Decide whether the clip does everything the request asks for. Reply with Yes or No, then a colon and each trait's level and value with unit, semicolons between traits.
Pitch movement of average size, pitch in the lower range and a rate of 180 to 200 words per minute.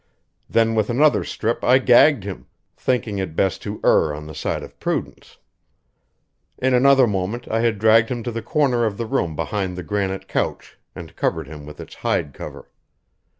Yes: average, 4.1 semitones; low, 110 Hz; average, 185 wpm